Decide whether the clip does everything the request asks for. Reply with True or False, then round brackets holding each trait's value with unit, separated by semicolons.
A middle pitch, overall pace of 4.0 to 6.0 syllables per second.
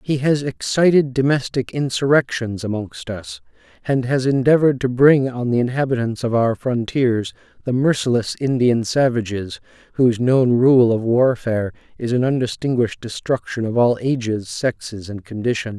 False (120 Hz; 4.9 syllables/s)